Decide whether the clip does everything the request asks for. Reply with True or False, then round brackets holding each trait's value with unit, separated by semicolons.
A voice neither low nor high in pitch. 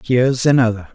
False (120 Hz)